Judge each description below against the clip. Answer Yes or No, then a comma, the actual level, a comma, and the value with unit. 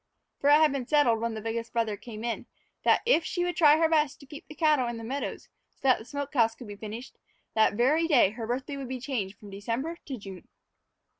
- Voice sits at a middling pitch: No, very high, 250 Hz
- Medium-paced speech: No, fast, 240 wpm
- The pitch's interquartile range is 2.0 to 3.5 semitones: No, average, 4.7 semitones